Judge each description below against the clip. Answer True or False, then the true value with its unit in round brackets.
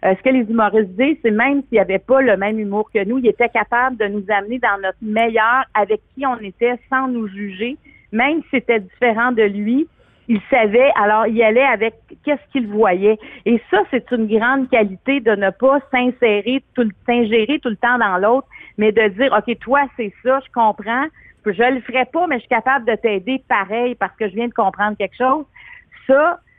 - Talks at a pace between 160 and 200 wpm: False (210 wpm)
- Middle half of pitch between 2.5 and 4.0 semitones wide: True (3.5 semitones)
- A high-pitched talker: True (235 Hz)